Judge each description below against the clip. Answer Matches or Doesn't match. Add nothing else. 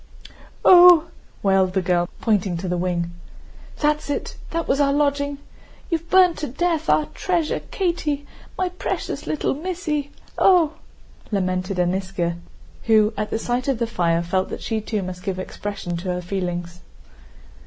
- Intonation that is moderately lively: Doesn't match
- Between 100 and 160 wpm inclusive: Matches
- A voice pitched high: Matches